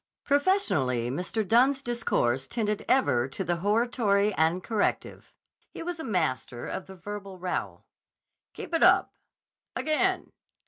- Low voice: No, high, 205 Hz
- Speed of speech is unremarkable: No, slow, 130 wpm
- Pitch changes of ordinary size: No, wide, 6.0 semitones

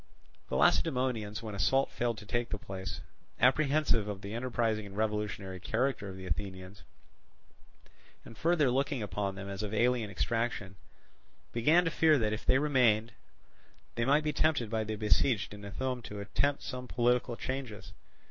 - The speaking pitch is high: No, low, 115 Hz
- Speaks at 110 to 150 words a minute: No, average, 160 wpm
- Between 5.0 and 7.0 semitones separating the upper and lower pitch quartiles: No, average, 4.0 semitones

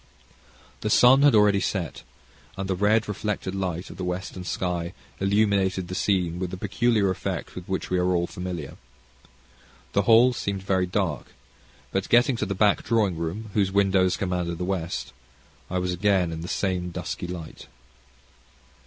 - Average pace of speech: Yes, average, 165 wpm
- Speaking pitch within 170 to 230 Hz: No, very low, 95 Hz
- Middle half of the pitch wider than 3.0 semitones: No, narrow, 2.4 semitones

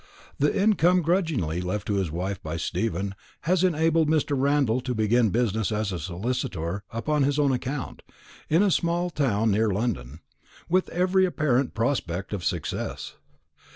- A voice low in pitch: Yes, low, 120 Hz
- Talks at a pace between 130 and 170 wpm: Yes, average, 155 wpm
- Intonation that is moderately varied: No, wide, 7.8 semitones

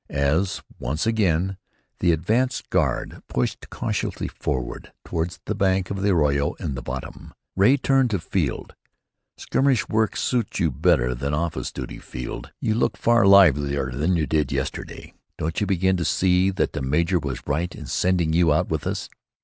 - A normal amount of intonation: Yes, average, 5.0 semitones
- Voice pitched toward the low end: Yes, very low, 85 Hz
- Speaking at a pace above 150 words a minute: Yes, average, 170 wpm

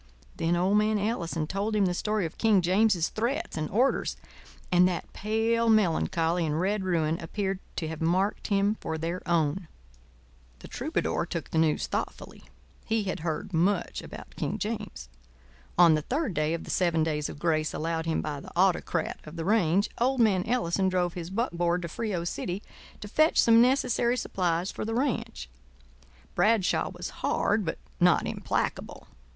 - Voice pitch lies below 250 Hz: Yes, medium, 185 Hz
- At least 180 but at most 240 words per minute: No, average, 170 wpm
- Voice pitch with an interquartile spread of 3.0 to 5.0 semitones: Yes, average, 4.5 semitones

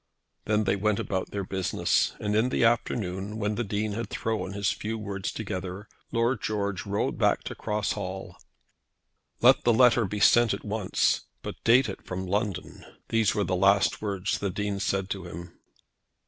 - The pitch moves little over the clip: Yes, narrow, 2.1 semitones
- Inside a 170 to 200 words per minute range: Yes, average, 180 wpm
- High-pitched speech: No, low, 105 Hz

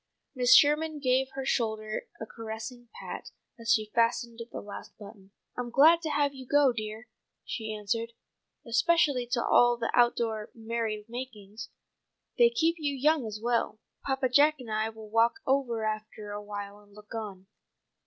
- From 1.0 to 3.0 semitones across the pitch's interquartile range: No, average, 3.6 semitones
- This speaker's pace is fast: No, average, 165 wpm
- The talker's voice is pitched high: Yes, high, 235 Hz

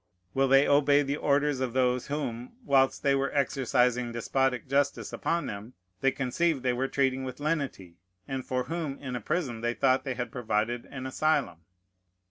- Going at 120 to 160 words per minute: No, average, 175 wpm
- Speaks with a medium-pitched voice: No, low, 130 Hz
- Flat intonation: Yes, narrow, 2.3 semitones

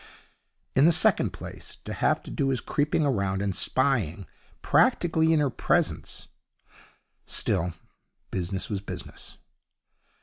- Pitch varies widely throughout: Yes, wide, 7.2 semitones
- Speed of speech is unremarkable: No, slow, 125 wpm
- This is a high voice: No, low, 125 Hz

